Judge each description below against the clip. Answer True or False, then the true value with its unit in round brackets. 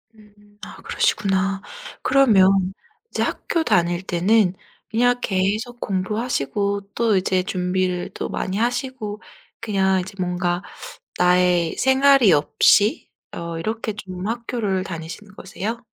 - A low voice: False (195 Hz)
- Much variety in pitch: False (3.5 semitones)